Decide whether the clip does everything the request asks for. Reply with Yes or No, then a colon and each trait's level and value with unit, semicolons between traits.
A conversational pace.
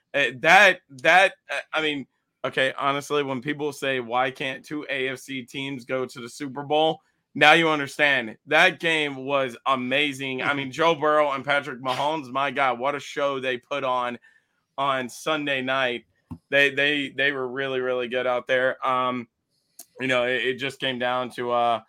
Yes: average, 175 wpm